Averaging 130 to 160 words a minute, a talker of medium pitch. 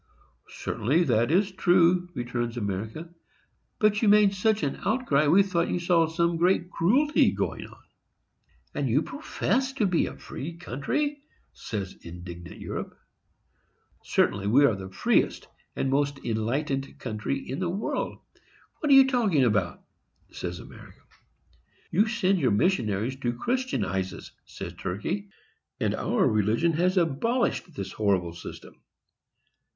Yes: slow, 135 wpm; medium, 155 Hz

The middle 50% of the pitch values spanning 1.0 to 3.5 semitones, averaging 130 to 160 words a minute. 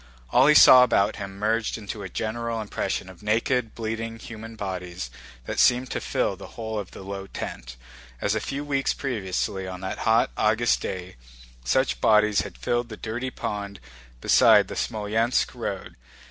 No: average, 3.0 semitones; average, 170 wpm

